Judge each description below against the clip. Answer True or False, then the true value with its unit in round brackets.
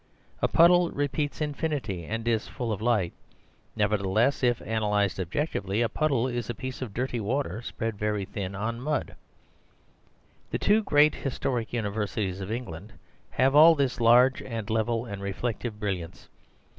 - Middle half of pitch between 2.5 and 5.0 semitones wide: True (4.2 semitones)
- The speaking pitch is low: True (115 Hz)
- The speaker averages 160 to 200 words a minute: False (150 wpm)